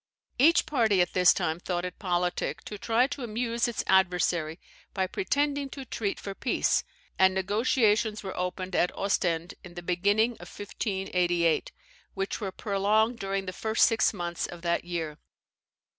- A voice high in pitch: Yes, high, 195 Hz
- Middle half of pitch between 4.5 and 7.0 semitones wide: No, average, 3.8 semitones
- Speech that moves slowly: No, average, 160 wpm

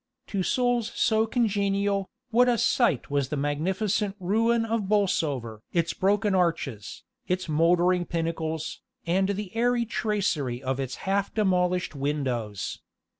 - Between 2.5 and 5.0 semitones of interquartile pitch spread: No, wide, 5.6 semitones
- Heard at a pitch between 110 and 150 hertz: No, medium, 185 Hz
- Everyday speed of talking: No, slow, 125 wpm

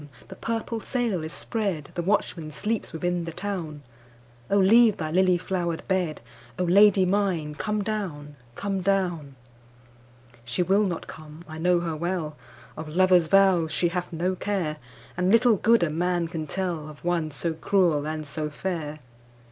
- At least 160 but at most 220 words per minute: No, average, 140 wpm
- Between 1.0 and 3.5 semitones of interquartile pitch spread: No, average, 3.9 semitones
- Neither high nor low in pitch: Yes, medium, 170 Hz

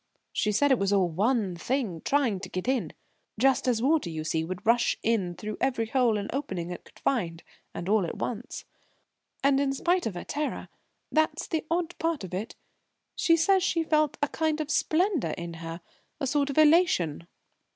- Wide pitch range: Yes, wide, 8.4 semitones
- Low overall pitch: No, high, 240 Hz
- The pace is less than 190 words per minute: No, average, 195 wpm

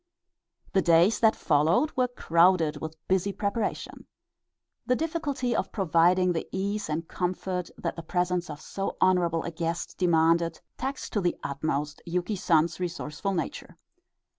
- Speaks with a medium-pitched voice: Yes, medium, 180 Hz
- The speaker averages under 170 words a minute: Yes, average, 140 wpm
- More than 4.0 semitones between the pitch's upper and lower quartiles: No, average, 3.3 semitones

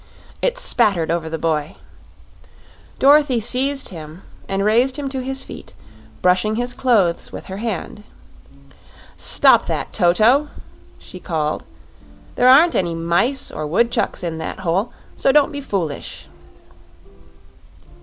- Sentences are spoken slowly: Yes, slow, 125 wpm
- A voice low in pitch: No, high, 215 Hz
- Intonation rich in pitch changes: Yes, wide, 7.7 semitones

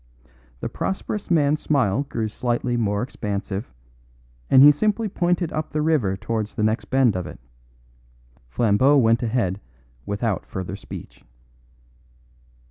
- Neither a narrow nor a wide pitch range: No, wide, 6.2 semitones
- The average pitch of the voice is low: Yes, low, 120 Hz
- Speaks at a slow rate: Yes, slow, 125 wpm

